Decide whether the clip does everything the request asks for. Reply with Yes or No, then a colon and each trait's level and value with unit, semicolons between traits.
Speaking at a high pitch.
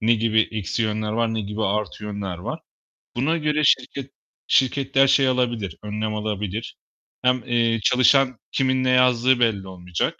No: low, 115 Hz